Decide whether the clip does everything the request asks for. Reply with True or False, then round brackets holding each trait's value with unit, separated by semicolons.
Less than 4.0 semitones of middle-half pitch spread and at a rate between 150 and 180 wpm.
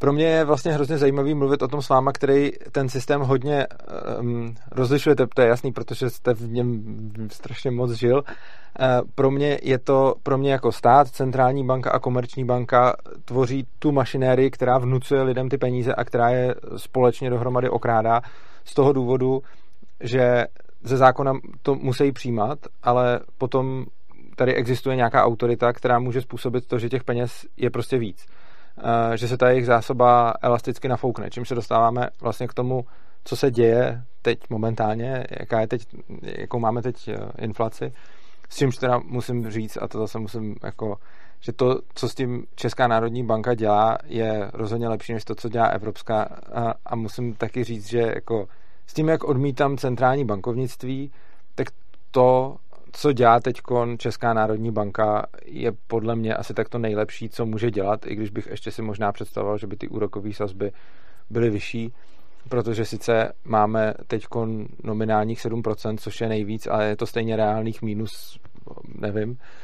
True (2.5 semitones; 165 wpm)